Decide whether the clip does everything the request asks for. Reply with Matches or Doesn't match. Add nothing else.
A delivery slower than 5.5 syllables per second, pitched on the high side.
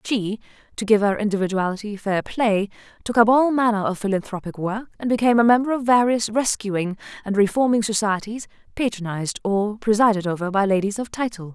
Doesn't match